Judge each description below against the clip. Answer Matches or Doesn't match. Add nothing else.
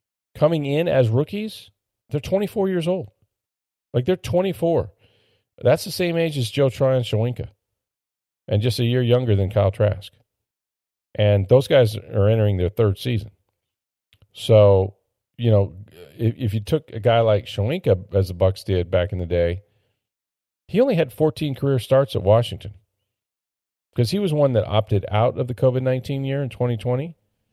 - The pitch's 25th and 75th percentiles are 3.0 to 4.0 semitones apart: Doesn't match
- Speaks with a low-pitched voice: Matches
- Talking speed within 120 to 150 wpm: Doesn't match